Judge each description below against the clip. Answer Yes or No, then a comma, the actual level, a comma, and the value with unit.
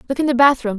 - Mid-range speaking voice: No, very high, 255 Hz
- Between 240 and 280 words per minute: No, fast, 305 wpm